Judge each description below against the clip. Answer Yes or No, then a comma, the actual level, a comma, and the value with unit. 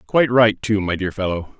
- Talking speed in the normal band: No, fast, 225 wpm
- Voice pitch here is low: Yes, low, 105 Hz